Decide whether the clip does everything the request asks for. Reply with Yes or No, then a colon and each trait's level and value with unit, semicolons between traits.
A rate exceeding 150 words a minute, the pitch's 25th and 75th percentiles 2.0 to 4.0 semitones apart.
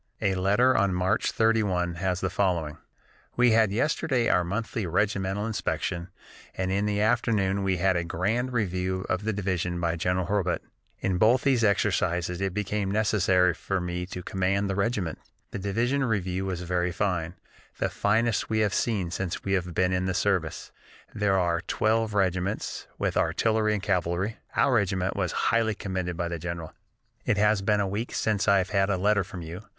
Yes: average, 180 wpm; average, 2.7 semitones